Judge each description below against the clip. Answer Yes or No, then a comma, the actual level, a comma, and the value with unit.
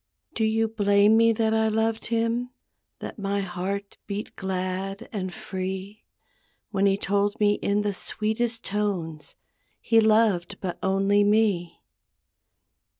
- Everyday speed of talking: No, slow, 130 wpm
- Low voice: No, high, 205 Hz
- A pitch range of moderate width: No, narrow, 2.3 semitones